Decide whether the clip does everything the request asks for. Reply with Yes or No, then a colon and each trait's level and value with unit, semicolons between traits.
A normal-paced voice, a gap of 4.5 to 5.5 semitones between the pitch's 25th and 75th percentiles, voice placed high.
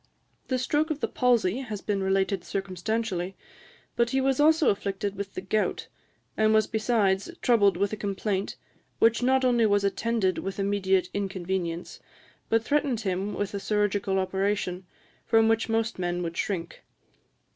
No: average, 155 wpm; average, 2.9 semitones; high, 205 Hz